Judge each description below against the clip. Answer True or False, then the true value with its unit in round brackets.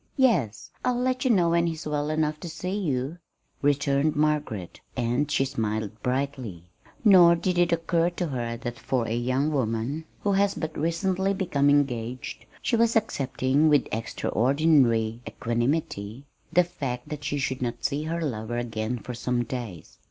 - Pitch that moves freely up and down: True (5.7 semitones)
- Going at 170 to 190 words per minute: False (160 wpm)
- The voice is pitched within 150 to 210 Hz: False (140 Hz)